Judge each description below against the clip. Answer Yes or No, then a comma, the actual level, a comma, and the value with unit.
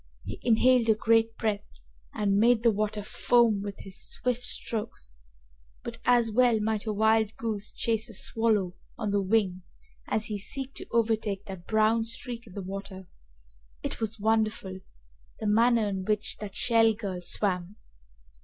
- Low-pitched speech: No, high, 220 Hz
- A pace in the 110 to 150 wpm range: No, average, 160 wpm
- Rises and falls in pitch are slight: Yes, narrow, 2.1 semitones